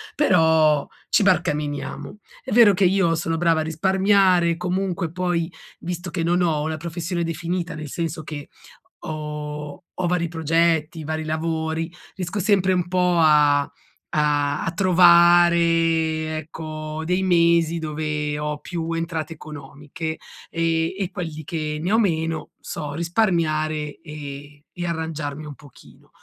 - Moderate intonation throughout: No, narrow, 2.2 semitones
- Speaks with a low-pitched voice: No, medium, 165 Hz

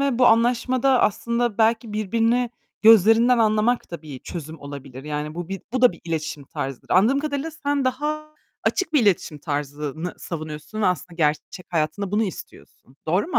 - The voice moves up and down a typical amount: No, wide, 7.7 semitones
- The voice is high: Yes, high, 210 Hz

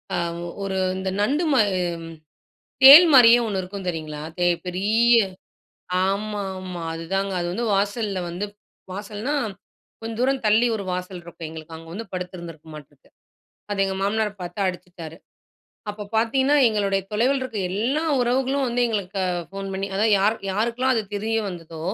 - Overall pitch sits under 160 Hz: No, high, 200 Hz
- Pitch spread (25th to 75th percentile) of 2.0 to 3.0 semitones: No, average, 4.0 semitones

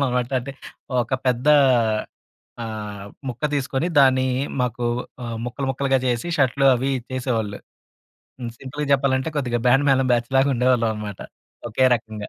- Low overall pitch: Yes, low, 125 Hz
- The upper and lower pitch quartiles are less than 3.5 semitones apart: Yes, narrow, 2.4 semitones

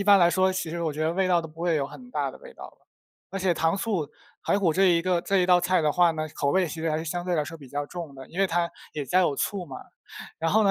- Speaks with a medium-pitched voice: Yes, medium, 170 Hz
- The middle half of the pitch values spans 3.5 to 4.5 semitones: No, average, 3.1 semitones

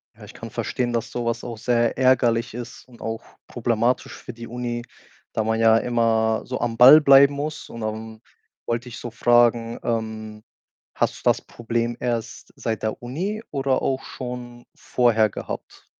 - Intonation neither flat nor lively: No, narrow, 1.6 semitones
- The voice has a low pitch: Yes, low, 120 Hz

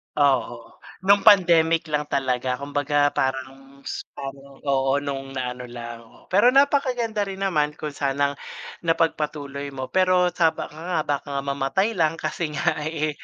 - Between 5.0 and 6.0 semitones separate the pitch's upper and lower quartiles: No, average, 3.8 semitones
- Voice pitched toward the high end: No, medium, 145 Hz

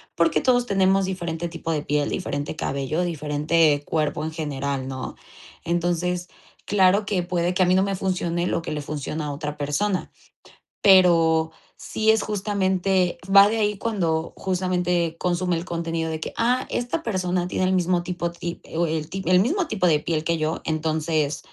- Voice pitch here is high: No, medium, 175 Hz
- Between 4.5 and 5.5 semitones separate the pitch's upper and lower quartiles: No, average, 3.0 semitones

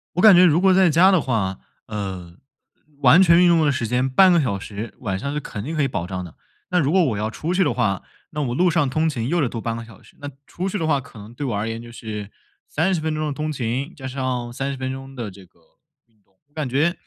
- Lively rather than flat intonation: Yes, wide, 6.0 semitones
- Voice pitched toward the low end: Yes, low, 130 Hz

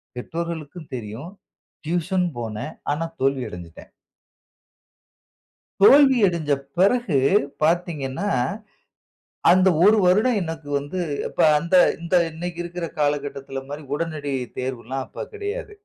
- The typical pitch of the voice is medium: Yes, medium, 165 Hz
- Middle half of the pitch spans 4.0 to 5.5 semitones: Yes, average, 4.6 semitones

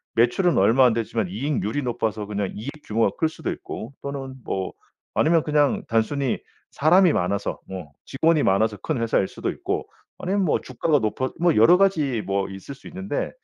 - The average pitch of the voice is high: No, low, 125 Hz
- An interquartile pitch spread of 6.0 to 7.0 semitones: Yes, wide, 6.3 semitones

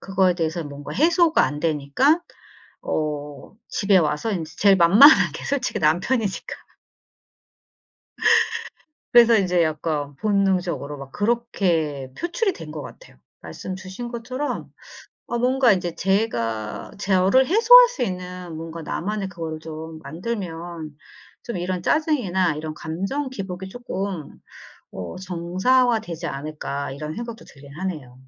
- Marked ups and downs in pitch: Yes, wide, 6.6 semitones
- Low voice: No, medium, 185 Hz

